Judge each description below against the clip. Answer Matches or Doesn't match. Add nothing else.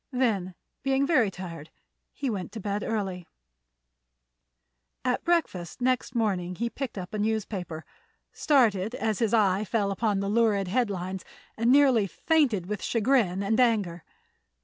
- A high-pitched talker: Matches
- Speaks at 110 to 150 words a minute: Matches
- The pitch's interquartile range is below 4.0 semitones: Doesn't match